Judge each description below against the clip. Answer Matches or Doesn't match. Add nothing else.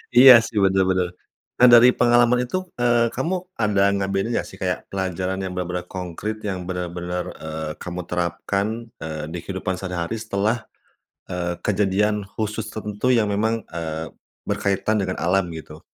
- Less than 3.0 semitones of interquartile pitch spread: Doesn't match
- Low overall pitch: Matches